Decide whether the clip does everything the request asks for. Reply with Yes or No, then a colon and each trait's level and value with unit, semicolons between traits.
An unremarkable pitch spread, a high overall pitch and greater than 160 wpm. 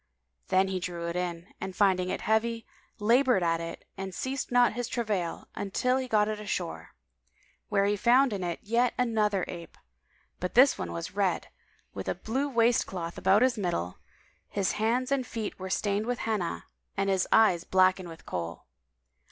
Yes: average, 4.7 semitones; high, 200 Hz; average, 175 wpm